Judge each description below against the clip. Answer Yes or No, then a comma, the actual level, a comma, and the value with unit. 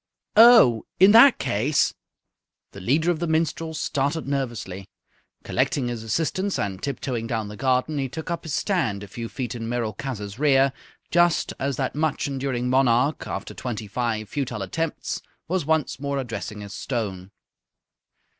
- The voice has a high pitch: No, low, 130 Hz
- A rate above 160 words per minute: No, average, 155 wpm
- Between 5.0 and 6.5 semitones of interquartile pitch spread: Yes, wide, 5.5 semitones